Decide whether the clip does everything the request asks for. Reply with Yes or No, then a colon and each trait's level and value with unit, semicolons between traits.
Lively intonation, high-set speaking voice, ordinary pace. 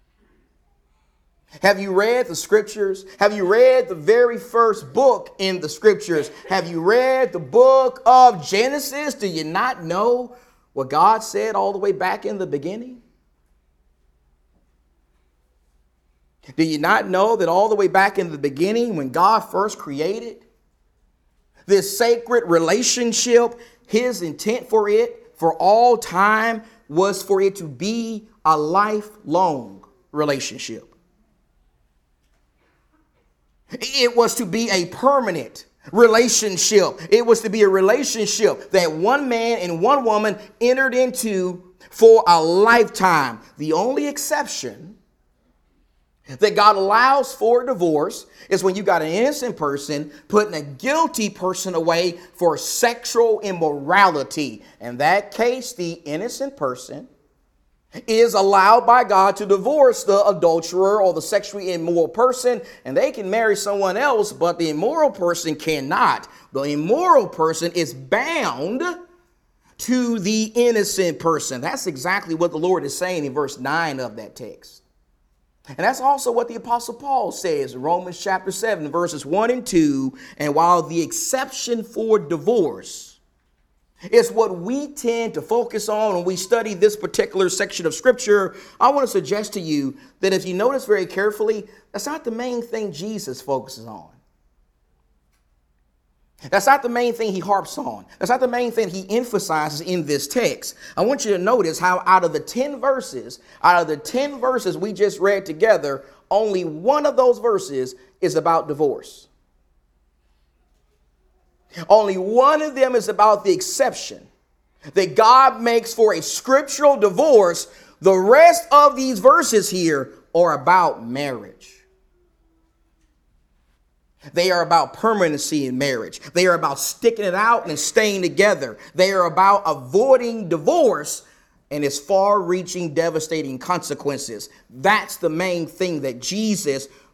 Yes: wide, 7.0 semitones; high, 195 Hz; average, 145 wpm